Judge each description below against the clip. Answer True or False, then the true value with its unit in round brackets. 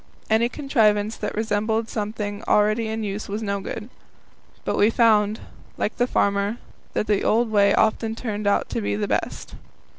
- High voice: True (215 Hz)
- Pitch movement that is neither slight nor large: False (1.5 semitones)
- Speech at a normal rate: True (170 wpm)